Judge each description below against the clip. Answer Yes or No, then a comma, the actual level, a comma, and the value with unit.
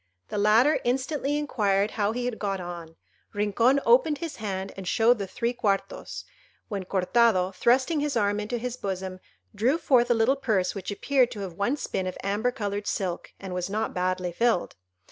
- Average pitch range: Yes, average, 4.3 semitones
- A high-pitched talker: Yes, high, 210 Hz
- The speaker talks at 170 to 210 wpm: Yes, average, 185 wpm